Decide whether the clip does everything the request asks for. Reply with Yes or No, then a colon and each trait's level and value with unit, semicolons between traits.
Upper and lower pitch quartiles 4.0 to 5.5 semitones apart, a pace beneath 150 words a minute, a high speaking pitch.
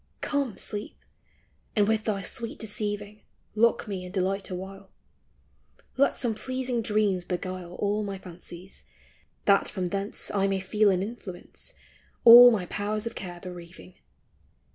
No: narrow, 2.6 semitones; average, 140 wpm; high, 200 Hz